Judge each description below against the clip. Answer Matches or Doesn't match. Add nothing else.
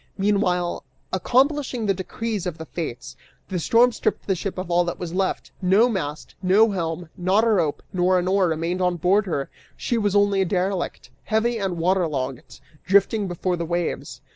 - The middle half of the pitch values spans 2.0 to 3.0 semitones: Matches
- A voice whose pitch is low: Doesn't match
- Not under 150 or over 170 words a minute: Doesn't match